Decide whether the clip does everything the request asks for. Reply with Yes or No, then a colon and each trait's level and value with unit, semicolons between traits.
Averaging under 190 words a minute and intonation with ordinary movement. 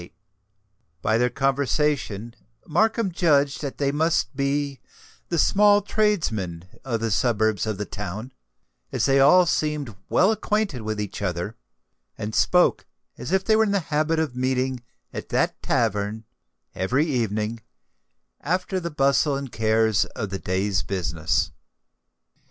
No: average, 140 wpm; wide, 6.4 semitones